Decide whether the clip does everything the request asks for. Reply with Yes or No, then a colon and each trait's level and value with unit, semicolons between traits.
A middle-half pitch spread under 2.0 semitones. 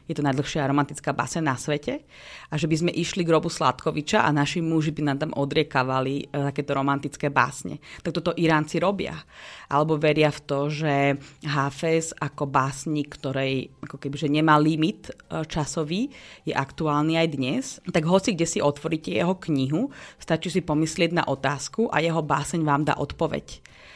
No: narrow, 2.6 semitones